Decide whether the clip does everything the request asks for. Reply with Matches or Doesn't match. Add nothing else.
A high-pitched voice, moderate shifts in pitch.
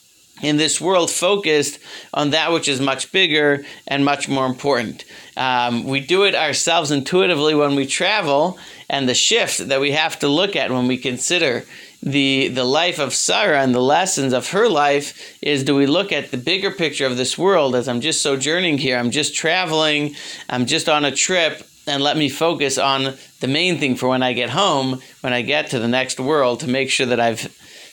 Doesn't match